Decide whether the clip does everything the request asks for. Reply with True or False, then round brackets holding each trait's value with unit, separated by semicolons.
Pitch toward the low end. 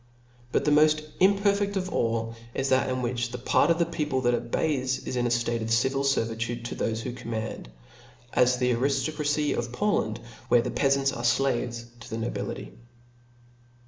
True (125 Hz)